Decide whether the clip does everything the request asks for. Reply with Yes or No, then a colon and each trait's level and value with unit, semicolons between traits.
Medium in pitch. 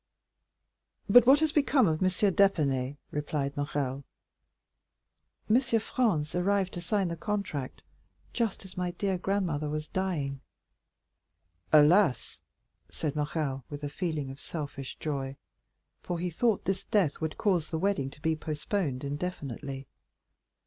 Yes: medium, 160 Hz